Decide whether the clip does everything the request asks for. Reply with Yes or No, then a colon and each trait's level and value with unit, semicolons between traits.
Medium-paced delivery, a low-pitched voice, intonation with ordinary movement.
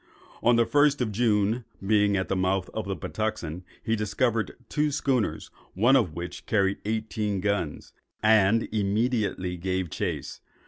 Yes: average, 145 wpm; low, 105 Hz; average, 3.2 semitones